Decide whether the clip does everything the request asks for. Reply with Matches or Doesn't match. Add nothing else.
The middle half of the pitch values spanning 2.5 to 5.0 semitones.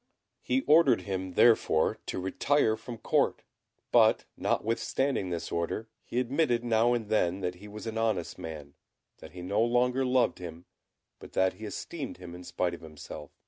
Doesn't match